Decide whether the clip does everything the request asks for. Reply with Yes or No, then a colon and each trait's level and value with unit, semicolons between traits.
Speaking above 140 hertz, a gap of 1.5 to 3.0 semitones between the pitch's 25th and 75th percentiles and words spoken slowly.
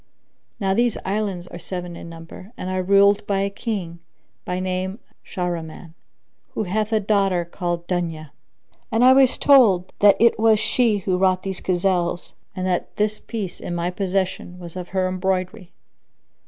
No: medium, 185 Hz; narrow, 2.6 semitones; average, 165 wpm